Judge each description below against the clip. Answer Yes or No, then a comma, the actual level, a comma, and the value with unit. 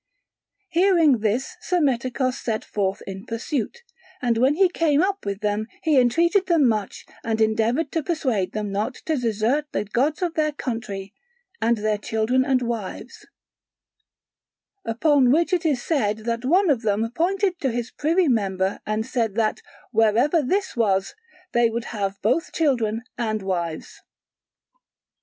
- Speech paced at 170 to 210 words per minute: No, average, 150 wpm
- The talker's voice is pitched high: Yes, high, 240 Hz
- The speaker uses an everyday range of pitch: No, wide, 6.0 semitones